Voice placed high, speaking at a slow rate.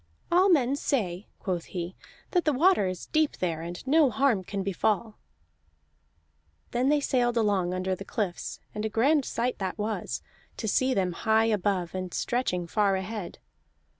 No: high, 210 Hz; average, 165 wpm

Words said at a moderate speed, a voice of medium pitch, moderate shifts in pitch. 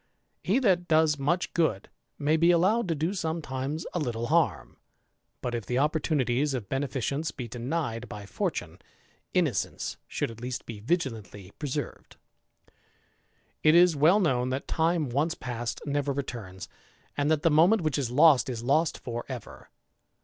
Yes: average, 155 wpm; medium, 145 Hz; average, 4.8 semitones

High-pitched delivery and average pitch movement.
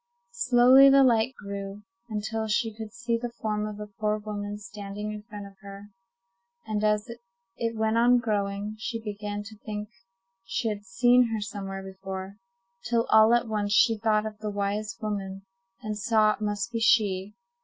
No: high, 210 Hz; narrow, 1.7 semitones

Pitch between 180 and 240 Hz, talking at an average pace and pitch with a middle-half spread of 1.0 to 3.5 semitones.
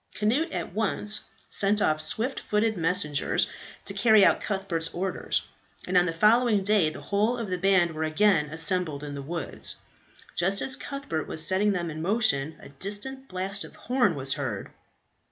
No: high, 190 Hz; average, 175 wpm; average, 4.7 semitones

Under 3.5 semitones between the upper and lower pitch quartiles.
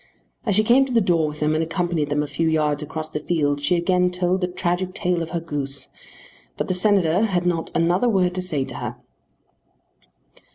Yes: average, 3.0 semitones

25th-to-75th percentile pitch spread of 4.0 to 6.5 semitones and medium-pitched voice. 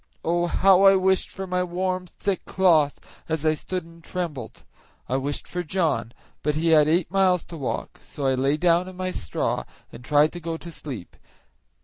No: average, 3.5 semitones; medium, 170 Hz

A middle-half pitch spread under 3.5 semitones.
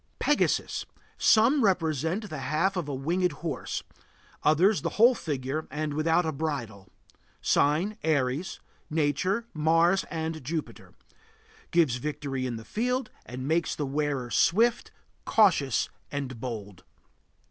No: average, 4.9 semitones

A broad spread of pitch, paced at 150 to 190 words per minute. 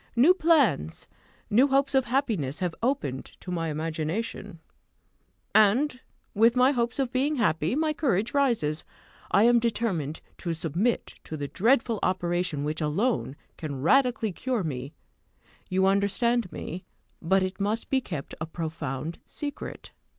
No: wide, 7.5 semitones; average, 140 wpm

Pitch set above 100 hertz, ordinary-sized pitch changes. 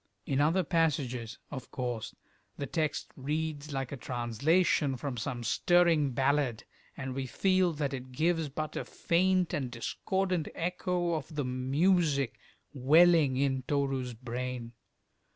Yes: medium, 140 Hz; average, 4.3 semitones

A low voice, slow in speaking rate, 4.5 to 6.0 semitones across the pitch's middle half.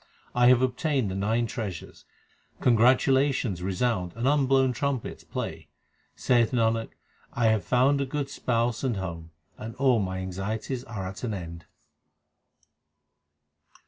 Yes: low, 115 Hz; slow, 130 wpm; average, 4.8 semitones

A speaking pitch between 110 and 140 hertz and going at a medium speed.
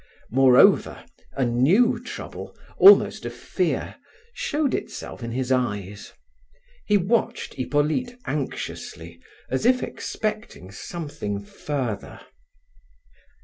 No: low, 135 Hz; slow, 95 wpm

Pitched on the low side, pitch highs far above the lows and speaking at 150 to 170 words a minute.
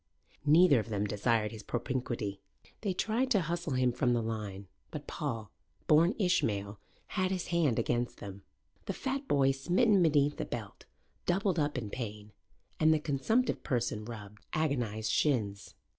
Yes: low, 130 Hz; wide, 7.7 semitones; average, 155 wpm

